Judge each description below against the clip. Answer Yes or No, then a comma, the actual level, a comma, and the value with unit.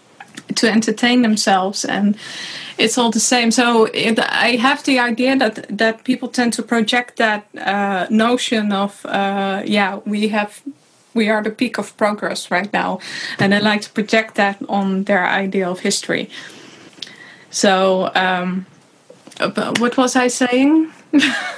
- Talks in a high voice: Yes, high, 220 Hz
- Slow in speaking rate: No, average, 150 wpm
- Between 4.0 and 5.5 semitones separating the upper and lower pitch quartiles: No, average, 3.5 semitones